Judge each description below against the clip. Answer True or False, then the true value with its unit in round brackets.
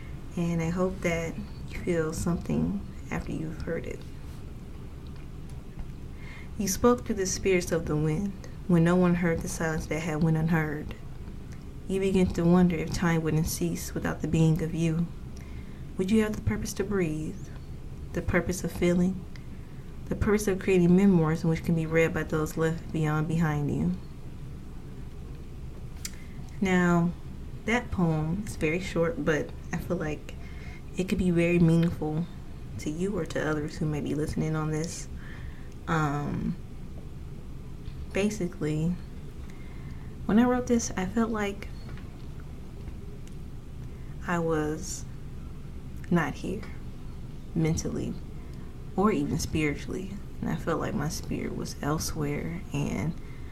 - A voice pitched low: False (160 Hz)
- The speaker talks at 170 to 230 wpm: False (135 wpm)